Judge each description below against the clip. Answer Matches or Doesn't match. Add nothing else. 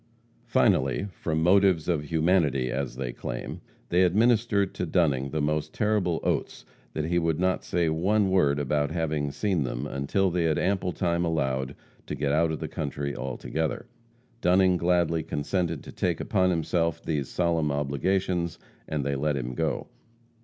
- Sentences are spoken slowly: Doesn't match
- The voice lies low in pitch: Matches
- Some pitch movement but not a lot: Matches